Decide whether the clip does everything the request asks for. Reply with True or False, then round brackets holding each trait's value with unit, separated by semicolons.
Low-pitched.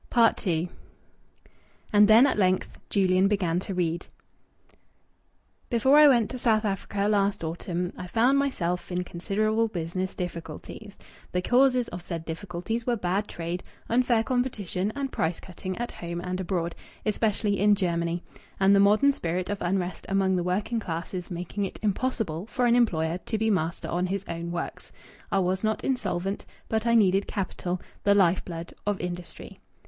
False (195 Hz)